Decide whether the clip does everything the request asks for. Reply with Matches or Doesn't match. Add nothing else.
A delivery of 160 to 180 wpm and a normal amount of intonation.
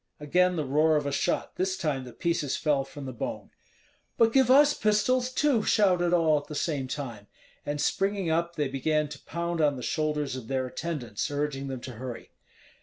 Doesn't match